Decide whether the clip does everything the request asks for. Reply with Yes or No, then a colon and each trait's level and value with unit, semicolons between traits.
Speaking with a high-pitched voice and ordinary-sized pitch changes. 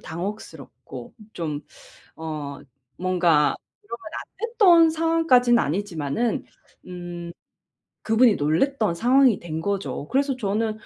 No: high, 205 Hz; wide, 7.2 semitones